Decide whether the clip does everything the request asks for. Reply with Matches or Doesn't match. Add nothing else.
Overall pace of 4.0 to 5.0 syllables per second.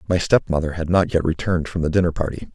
Doesn't match